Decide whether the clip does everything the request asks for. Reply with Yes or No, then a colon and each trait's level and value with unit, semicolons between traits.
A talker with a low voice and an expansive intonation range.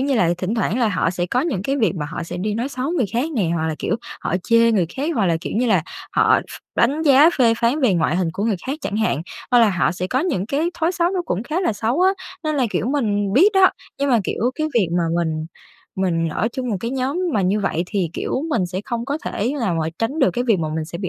No: high, 230 Hz; wide, 6.9 semitones